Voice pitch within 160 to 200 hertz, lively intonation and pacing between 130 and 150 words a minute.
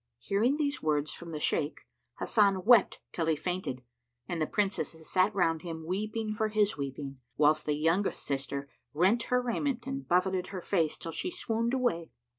No: medium, 185 Hz; wide, 5.7 semitones; average, 175 wpm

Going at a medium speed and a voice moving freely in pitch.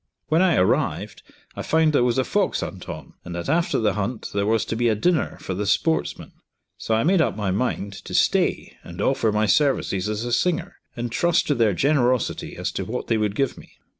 No: fast, 225 wpm; wide, 6.6 semitones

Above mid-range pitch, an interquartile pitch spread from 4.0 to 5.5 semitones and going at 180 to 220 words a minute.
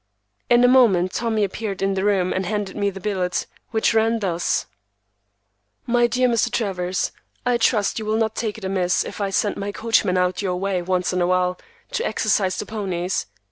No: high, 200 Hz; average, 3.4 semitones; average, 190 wpm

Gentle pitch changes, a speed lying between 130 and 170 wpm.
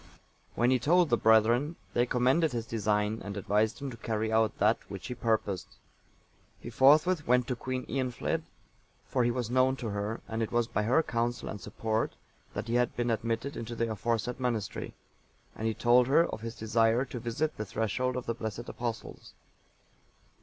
No: narrow, 2.2 semitones; average, 185 wpm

